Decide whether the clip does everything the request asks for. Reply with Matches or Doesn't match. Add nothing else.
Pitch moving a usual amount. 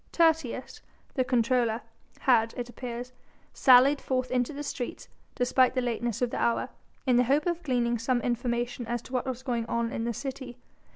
Doesn't match